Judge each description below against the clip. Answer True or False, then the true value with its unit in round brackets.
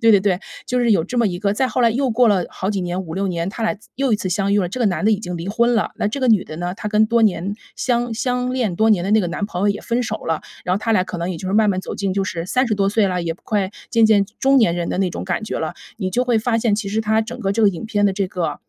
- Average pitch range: True (3.5 semitones)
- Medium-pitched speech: False (205 Hz)